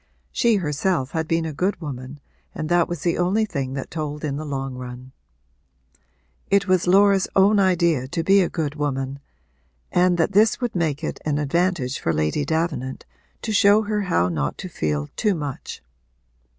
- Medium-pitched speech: Yes, medium, 160 Hz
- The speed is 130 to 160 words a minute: No, average, 175 wpm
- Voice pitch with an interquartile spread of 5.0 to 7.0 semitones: Yes, wide, 5.4 semitones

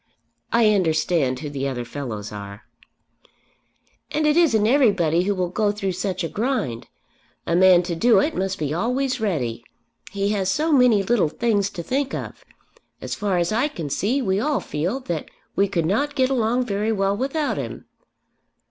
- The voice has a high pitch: Yes, high, 200 Hz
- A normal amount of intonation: No, wide, 6.5 semitones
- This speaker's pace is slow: No, average, 175 wpm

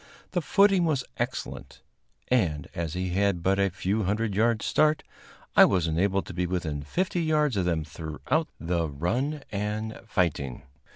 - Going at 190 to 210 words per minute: No, average, 160 wpm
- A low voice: Yes, low, 100 Hz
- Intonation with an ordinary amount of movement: No, wide, 6.9 semitones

